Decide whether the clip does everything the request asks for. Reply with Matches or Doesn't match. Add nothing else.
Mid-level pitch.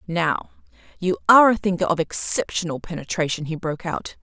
Matches